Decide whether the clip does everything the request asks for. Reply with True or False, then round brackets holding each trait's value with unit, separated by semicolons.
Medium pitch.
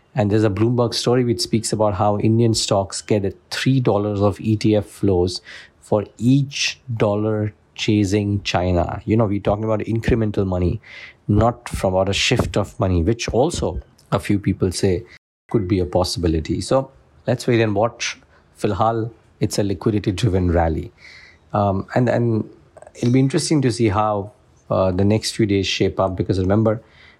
False (105 Hz)